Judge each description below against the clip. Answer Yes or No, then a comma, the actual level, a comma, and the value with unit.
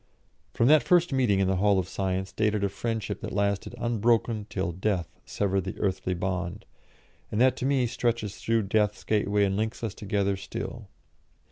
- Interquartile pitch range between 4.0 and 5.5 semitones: No, average, 3.0 semitones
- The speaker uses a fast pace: No, average, 175 wpm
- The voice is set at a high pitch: No, low, 105 Hz